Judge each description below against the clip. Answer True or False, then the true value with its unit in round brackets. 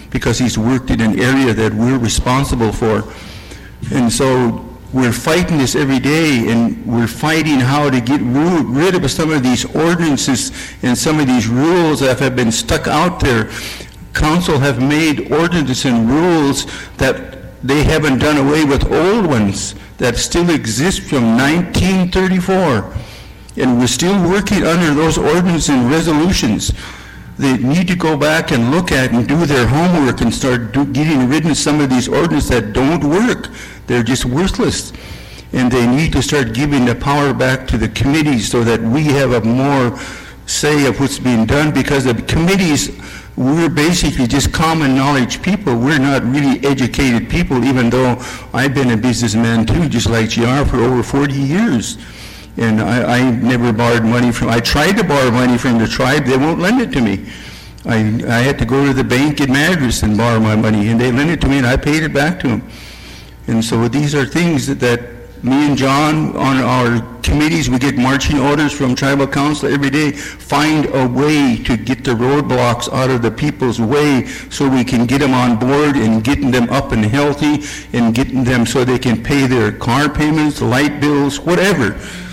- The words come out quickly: False (185 wpm)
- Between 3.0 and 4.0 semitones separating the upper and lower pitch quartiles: True (3.6 semitones)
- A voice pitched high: False (130 Hz)